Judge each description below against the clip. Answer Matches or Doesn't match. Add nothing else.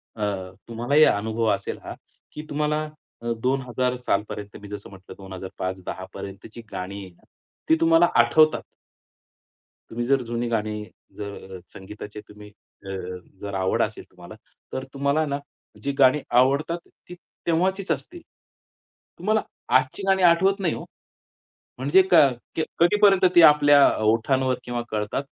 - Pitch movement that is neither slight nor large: Doesn't match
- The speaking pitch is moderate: Doesn't match